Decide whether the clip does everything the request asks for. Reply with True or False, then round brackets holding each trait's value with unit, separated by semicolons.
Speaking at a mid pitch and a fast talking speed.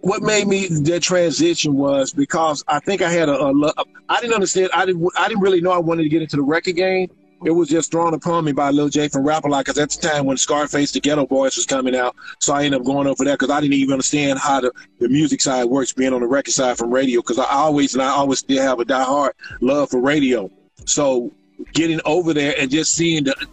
True (150 Hz; 260 wpm)